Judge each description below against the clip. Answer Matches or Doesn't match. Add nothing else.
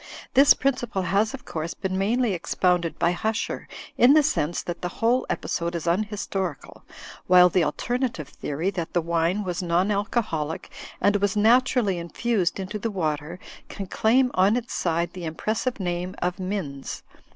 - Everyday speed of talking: Matches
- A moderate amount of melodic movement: Matches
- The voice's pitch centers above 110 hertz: Matches